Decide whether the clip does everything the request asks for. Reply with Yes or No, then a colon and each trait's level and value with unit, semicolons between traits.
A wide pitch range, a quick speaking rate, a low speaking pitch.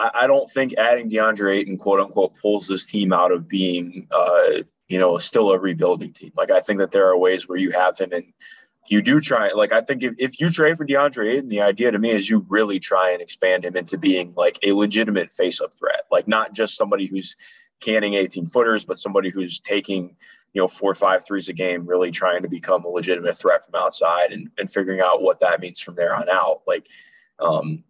Yes: wide, 6.4 semitones; fast, 230 wpm; low, 100 Hz